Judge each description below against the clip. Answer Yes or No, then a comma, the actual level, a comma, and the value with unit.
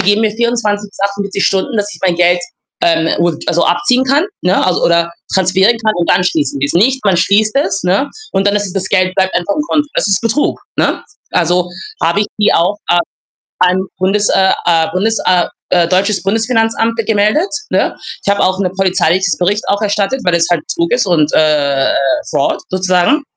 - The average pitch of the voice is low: No, high, 190 Hz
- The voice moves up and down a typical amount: Yes, average, 3.1 semitones